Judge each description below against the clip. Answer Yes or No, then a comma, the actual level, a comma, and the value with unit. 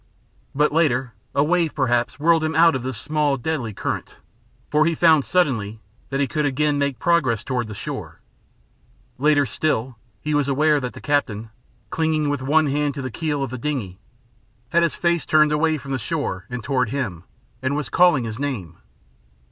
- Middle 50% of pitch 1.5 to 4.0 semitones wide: Yes, average, 3.7 semitones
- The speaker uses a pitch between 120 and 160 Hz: Yes, medium, 140 Hz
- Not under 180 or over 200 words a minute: Yes, average, 185 wpm